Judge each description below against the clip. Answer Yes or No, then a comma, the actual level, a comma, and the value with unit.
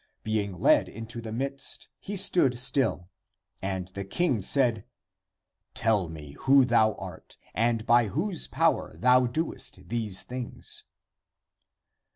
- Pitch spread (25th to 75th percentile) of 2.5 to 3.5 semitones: No, average, 4.3 semitones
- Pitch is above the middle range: No, low, 115 Hz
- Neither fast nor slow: No, slow, 130 wpm